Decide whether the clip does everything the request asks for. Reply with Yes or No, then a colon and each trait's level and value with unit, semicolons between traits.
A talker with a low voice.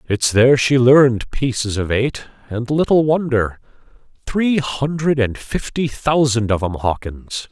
Yes: low, 125 Hz